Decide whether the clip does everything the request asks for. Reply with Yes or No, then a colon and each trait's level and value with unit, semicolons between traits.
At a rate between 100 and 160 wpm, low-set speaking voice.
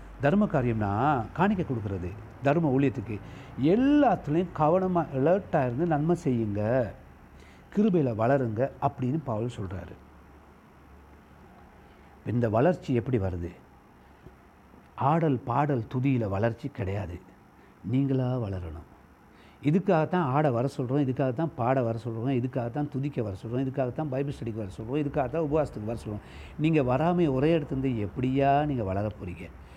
Yes: average, 115 wpm; low, 130 Hz